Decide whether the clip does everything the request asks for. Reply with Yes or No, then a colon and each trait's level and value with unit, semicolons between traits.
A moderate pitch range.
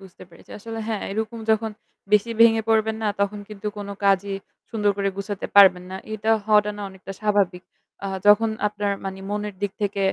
No: narrow, 1.6 semitones